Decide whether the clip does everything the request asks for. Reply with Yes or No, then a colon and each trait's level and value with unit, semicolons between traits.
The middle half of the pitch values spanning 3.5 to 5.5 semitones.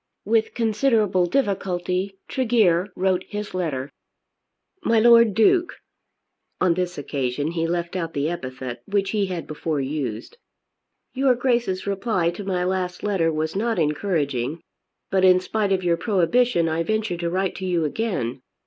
Yes: average, 4.2 semitones